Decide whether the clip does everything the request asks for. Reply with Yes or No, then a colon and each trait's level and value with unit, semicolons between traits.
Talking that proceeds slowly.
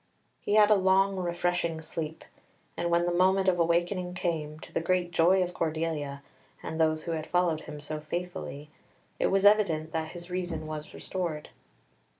No: average, 170 wpm